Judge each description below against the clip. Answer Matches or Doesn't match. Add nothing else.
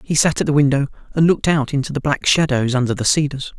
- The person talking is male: Matches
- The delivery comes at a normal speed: Doesn't match